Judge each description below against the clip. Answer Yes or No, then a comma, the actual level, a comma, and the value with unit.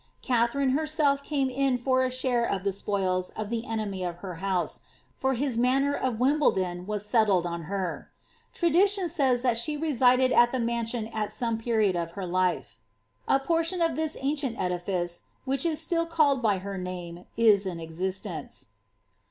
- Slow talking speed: No, average, 150 wpm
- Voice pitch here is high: Yes, high, 235 Hz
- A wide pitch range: Yes, wide, 6.5 semitones